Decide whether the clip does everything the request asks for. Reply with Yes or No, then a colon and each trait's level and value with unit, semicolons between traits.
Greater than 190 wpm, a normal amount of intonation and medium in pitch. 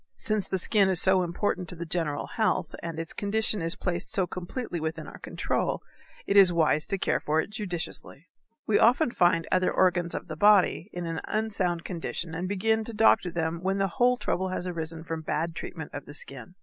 Yes: fast, 205 wpm; average, 3.3 semitones; medium, 180 Hz